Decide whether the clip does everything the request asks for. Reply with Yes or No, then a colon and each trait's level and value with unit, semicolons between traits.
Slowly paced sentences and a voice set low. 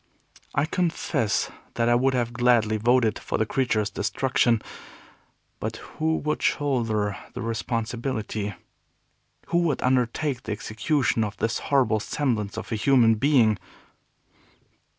Yes: slow, 125 wpm; low, 120 Hz